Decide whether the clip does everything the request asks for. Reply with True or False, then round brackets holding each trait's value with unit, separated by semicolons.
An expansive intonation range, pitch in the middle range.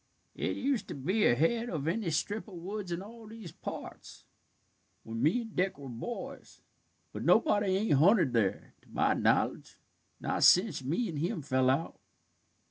True (6.9 semitones; 180 Hz)